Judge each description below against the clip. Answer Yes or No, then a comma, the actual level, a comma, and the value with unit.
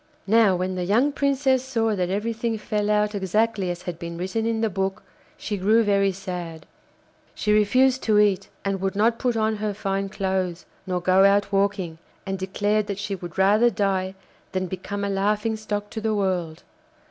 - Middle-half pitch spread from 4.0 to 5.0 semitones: No, narrow, 2.4 semitones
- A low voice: No, high, 200 Hz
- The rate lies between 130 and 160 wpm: No, average, 185 wpm